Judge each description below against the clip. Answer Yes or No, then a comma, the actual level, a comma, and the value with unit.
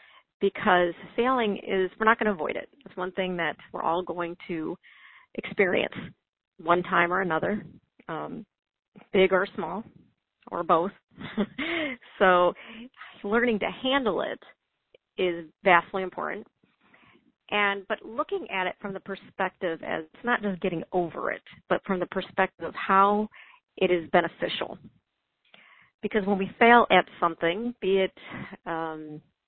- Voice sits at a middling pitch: No, high, 195 Hz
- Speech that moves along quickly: No, average, 140 wpm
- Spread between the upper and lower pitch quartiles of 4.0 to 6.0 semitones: No, average, 3.5 semitones